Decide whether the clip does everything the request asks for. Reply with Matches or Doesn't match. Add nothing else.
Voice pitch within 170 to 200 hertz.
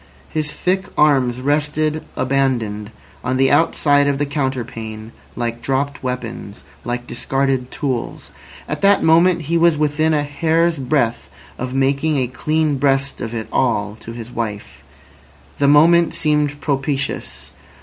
Doesn't match